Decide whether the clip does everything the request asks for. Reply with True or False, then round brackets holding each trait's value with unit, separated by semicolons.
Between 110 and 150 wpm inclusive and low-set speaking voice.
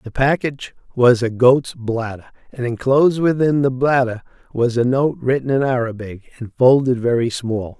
False (160 wpm; 125 Hz)